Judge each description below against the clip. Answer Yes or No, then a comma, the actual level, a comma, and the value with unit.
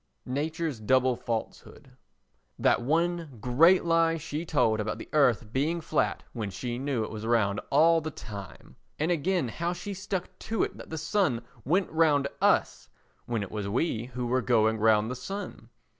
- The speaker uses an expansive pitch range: Yes, wide, 6.3 semitones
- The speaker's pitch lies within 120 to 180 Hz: Yes, medium, 140 Hz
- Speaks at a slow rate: No, average, 175 wpm